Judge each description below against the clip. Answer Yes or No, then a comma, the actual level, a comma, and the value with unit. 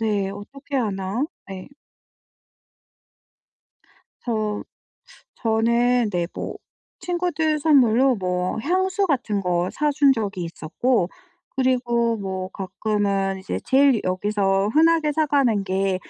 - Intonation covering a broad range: Yes, wide, 6.1 semitones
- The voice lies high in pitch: Yes, high, 225 Hz